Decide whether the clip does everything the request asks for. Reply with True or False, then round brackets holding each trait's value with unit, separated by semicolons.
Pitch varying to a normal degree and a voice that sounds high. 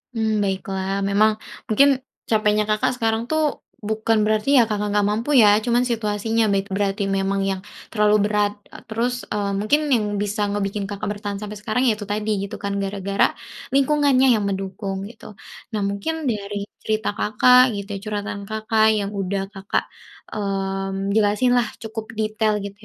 False (1.7 semitones; 210 Hz)